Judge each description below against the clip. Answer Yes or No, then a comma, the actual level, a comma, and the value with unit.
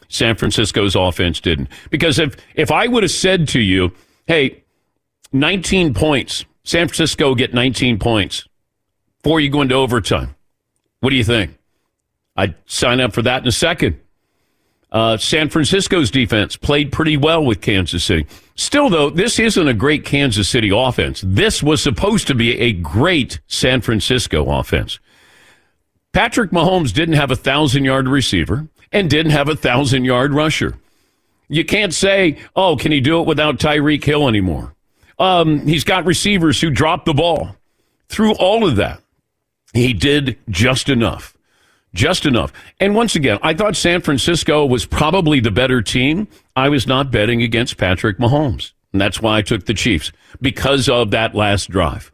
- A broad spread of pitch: Yes, wide, 5.7 semitones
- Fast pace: No, average, 165 wpm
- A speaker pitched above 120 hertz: Yes, low, 135 Hz